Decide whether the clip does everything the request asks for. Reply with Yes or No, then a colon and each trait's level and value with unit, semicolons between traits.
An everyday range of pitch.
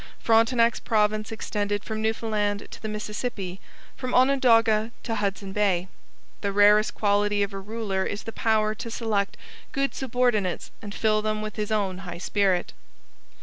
No: narrow, 1.8 semitones